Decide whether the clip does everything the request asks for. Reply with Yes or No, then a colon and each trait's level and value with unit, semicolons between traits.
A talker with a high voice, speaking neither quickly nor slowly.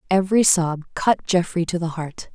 No: medium, 175 Hz; average, 180 wpm